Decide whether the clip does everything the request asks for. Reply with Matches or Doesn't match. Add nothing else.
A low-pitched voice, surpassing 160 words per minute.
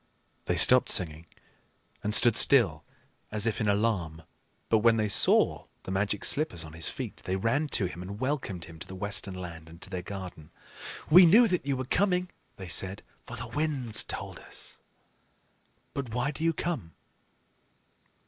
Matches